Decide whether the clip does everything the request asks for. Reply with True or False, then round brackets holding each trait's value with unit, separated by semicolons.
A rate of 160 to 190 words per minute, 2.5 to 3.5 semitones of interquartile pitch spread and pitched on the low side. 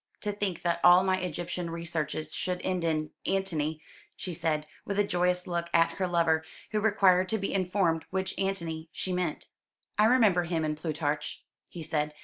False (175 wpm; 2.8 semitones; 175 Hz)